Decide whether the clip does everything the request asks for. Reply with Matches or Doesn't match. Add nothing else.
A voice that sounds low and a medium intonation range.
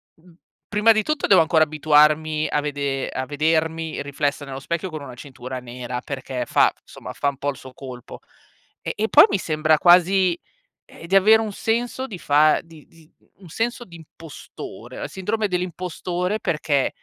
Doesn't match